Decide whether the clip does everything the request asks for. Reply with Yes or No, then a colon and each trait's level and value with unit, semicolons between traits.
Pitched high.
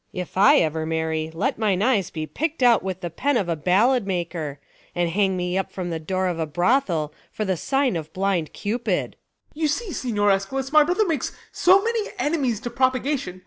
Yes: high, 195 Hz